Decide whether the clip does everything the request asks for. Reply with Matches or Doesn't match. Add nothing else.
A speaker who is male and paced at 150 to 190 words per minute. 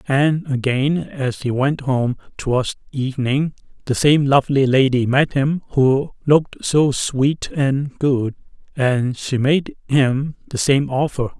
Doesn't match